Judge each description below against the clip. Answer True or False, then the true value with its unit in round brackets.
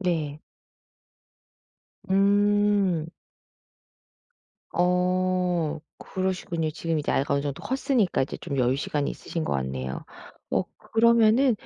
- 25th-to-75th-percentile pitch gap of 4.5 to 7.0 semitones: True (5.3 semitones)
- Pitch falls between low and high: True (180 Hz)